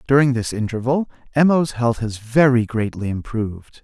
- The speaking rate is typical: Yes, average, 155 wpm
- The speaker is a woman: No, male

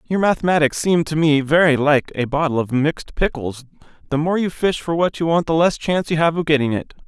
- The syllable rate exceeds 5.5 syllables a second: Yes, 5.9 syllables/s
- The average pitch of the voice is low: No, medium, 155 Hz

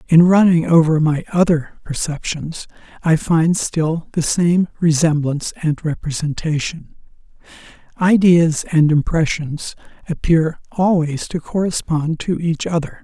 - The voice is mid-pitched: Yes, medium, 160 Hz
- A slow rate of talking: Yes, slow, 110 wpm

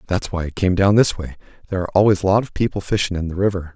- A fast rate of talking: Yes, fast, 290 wpm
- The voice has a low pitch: Yes, very low, 95 Hz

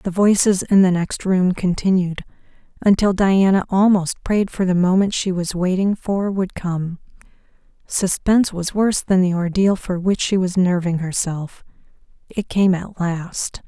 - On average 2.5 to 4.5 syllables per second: Yes, 4.4 syllables/s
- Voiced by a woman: Yes, female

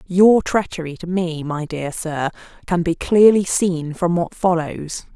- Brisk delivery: No, average, 165 wpm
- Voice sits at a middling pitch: Yes, medium, 175 Hz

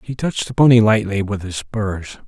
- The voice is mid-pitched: No, low, 110 Hz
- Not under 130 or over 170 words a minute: No, fast, 210 wpm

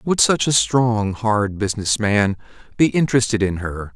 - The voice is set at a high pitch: No, low, 110 Hz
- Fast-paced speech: No, average, 165 wpm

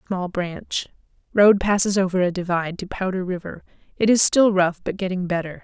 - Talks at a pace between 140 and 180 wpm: Yes, average, 170 wpm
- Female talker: Yes, female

